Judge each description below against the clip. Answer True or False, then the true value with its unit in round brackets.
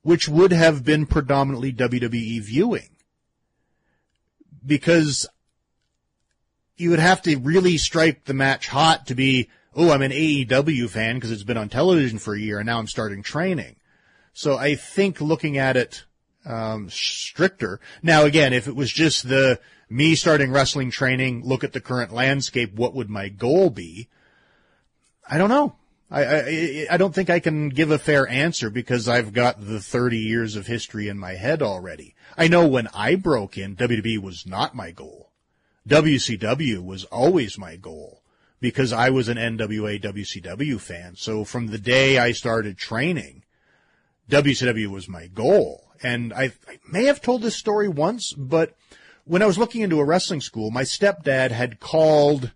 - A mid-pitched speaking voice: False (130 Hz)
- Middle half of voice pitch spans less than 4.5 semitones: False (5.3 semitones)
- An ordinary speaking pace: True (170 wpm)